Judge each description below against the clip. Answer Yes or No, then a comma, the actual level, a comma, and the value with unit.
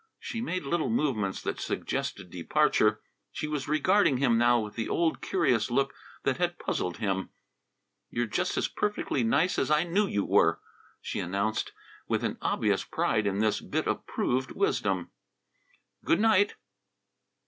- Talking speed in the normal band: Yes, average, 155 wpm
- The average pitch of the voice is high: No, low, 135 Hz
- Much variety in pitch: Yes, wide, 8.1 semitones